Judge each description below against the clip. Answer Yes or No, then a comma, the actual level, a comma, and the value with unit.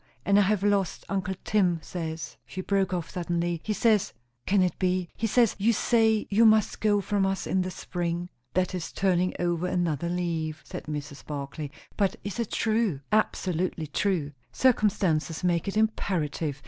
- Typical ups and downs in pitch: Yes, average, 3.3 semitones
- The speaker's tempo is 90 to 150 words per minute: No, average, 170 wpm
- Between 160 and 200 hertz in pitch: Yes, medium, 185 Hz